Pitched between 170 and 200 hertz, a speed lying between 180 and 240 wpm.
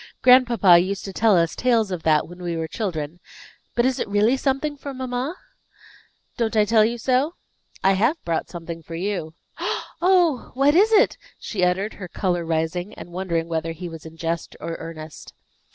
Yes: high, 190 Hz; average, 185 wpm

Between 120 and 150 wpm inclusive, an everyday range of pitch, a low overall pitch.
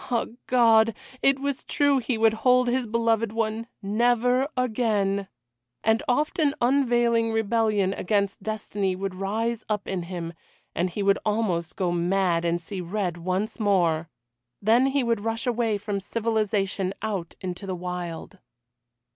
No: average, 145 wpm; average, 3.5 semitones; high, 215 Hz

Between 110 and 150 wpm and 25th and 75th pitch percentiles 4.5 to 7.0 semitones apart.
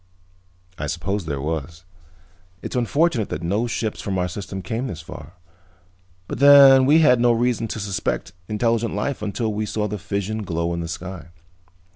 No: average, 170 wpm; average, 5.3 semitones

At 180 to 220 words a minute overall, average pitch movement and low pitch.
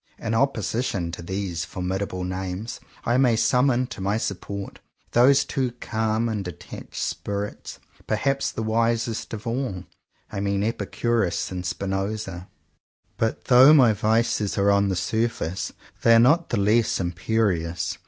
No: average, 145 wpm; average, 3.5 semitones; low, 110 Hz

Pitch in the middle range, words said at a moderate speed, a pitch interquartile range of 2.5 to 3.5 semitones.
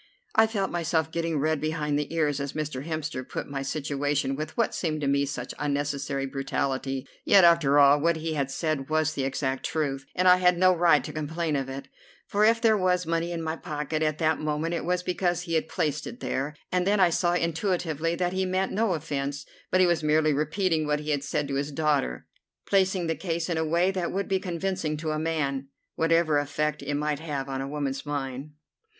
No: medium, 155 Hz; fast, 215 wpm; average, 3.2 semitones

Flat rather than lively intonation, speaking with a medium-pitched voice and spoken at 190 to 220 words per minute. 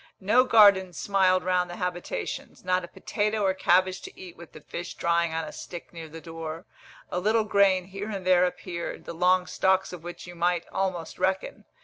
Yes: narrow, 1.8 semitones; medium, 180 Hz; average, 200 wpm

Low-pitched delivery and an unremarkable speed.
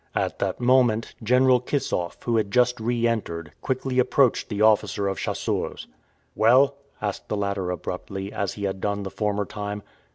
Yes: low, 110 Hz; average, 165 wpm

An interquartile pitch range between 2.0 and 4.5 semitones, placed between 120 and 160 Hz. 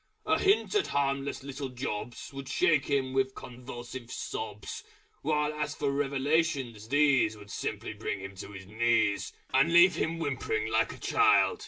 Yes: average, 3.8 semitones; low, 135 Hz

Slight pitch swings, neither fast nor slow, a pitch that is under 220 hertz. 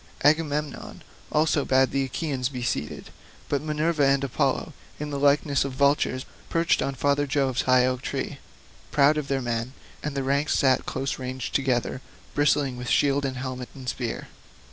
Yes: narrow, 2.1 semitones; average, 165 wpm; low, 135 Hz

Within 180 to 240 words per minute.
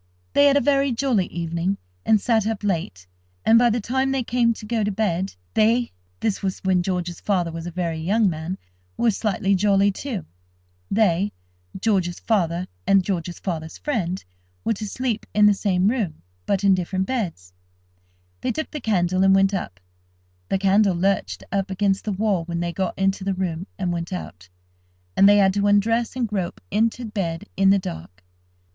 Yes: average, 185 wpm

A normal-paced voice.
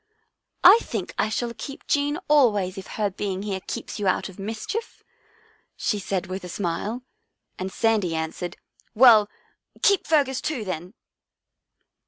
Yes: average, 155 wpm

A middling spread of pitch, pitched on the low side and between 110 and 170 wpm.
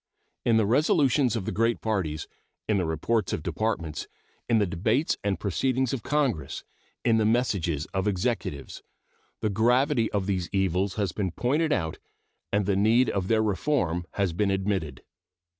Yes: average, 4.1 semitones; low, 105 Hz; average, 160 wpm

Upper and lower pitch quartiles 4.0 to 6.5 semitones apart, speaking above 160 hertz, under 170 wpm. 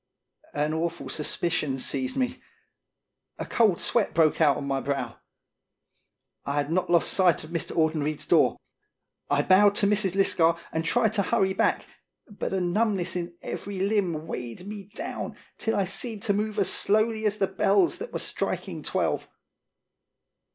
Yes: average, 4.6 semitones; medium, 185 Hz; average, 160 wpm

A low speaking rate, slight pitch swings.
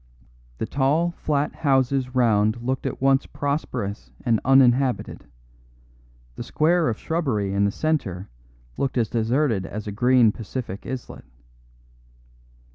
No: slow, 120 wpm; average, 4.3 semitones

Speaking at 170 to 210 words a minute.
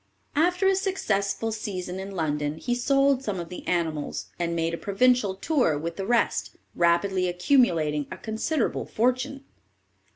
No: average, 150 wpm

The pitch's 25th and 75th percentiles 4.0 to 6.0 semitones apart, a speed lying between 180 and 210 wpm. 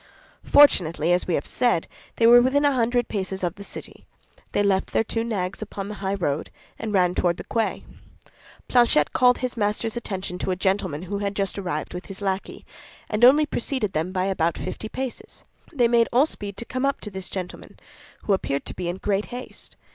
Yes: average, 4.4 semitones; fast, 205 wpm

